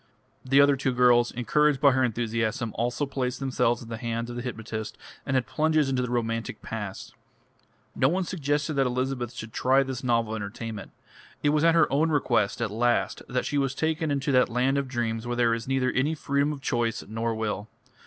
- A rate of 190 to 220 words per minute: Yes, fast, 205 wpm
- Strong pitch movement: No, average, 3.2 semitones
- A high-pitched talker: No, low, 125 Hz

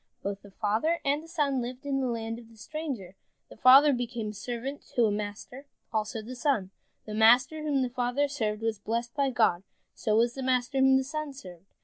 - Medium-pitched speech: No, high, 245 Hz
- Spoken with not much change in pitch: No, average, 4.0 semitones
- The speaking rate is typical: No, fast, 215 wpm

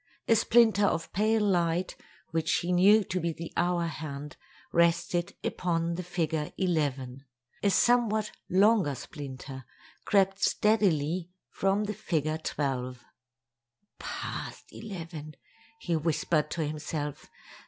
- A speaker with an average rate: No, slow, 115 wpm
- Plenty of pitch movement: No, average, 4.2 semitones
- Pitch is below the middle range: No, medium, 170 Hz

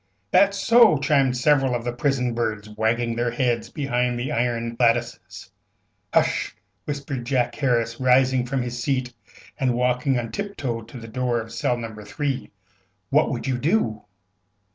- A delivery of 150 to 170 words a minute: Yes, average, 160 wpm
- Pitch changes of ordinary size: No, narrow, 2.3 semitones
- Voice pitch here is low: Yes, low, 125 Hz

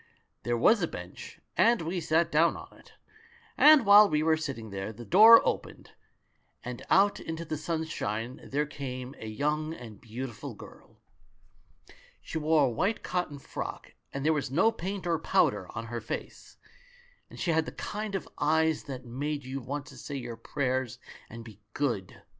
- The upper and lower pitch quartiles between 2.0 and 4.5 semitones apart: No, average, 5.3 semitones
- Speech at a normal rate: Yes, average, 175 wpm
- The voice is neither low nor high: Yes, medium, 145 Hz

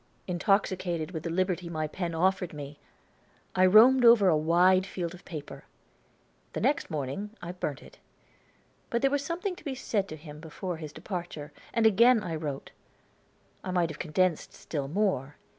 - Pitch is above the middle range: No, medium, 180 Hz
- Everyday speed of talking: Yes, average, 170 wpm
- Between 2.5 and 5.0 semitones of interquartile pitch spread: Yes, average, 4.3 semitones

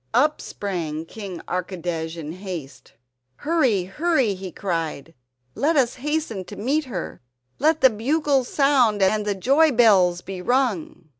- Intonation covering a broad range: Yes, wide, 7.3 semitones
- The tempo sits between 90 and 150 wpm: Yes, average, 140 wpm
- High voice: Yes, high, 210 Hz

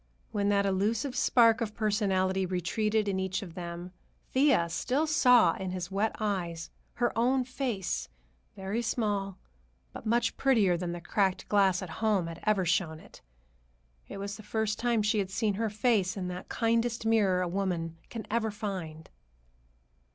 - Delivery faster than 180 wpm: No, average, 165 wpm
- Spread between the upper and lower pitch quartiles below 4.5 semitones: Yes, average, 3.5 semitones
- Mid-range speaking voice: No, high, 200 Hz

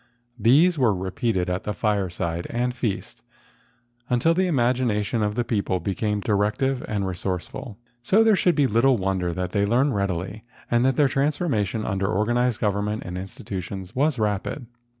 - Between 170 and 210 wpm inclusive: No, average, 160 wpm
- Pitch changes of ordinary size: Yes, average, 4.6 semitones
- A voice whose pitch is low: Yes, low, 105 Hz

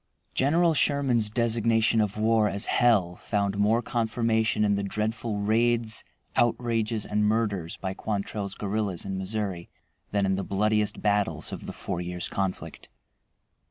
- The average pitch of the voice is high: No, low, 105 Hz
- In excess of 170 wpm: No, average, 140 wpm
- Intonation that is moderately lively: No, narrow, 2.3 semitones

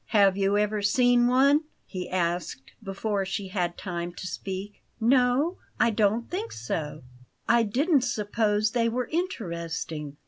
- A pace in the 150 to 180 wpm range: No, average, 140 wpm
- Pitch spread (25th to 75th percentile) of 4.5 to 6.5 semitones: Yes, average, 4.8 semitones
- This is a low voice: No, high, 210 Hz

